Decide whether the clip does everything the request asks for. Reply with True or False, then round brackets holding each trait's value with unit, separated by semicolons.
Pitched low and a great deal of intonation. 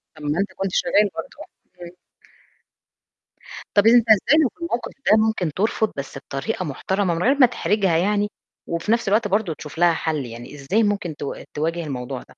False (190 Hz; 5.7 semitones)